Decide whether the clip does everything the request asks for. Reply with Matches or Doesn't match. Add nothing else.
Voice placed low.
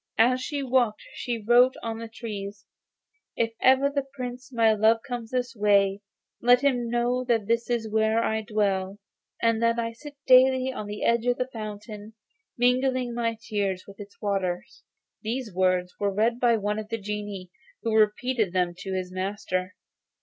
Doesn't match